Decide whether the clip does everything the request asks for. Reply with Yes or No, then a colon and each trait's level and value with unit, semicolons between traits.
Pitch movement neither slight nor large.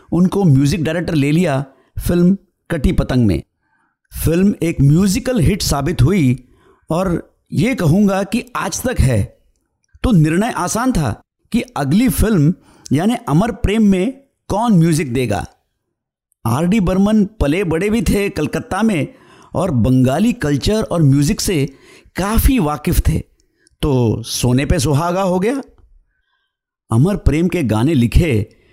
No: wide, 6.8 semitones